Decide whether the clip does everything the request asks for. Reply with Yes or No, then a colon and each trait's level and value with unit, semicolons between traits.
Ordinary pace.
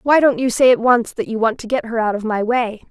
No: fast, 330 wpm